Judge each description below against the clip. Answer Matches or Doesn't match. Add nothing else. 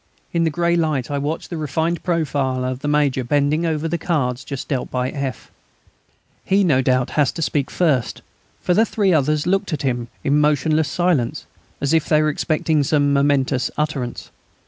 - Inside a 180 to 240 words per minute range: Matches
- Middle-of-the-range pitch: Matches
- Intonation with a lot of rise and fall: Doesn't match